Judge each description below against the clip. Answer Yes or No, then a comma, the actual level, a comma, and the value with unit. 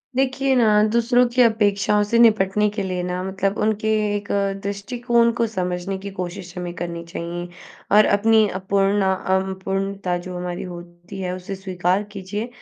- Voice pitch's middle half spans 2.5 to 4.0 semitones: Yes, average, 3.1 semitones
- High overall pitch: Yes, high, 195 Hz